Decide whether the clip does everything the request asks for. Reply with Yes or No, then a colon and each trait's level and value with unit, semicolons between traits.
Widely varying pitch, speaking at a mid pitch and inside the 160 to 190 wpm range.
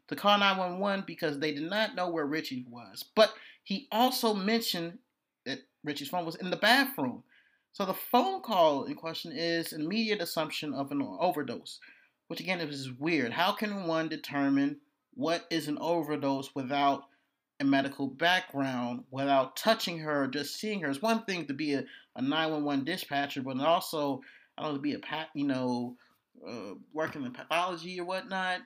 Yes: wide, 7.3 semitones; medium, 165 Hz; average, 170 wpm